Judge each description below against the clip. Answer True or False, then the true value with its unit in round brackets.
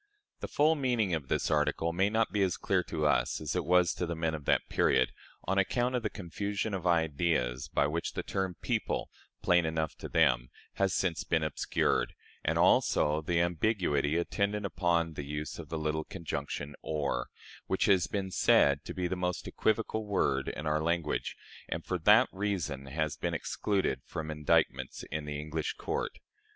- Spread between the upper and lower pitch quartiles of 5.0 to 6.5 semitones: False (4.2 semitones)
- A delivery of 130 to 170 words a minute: False (185 wpm)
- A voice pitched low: True (85 Hz)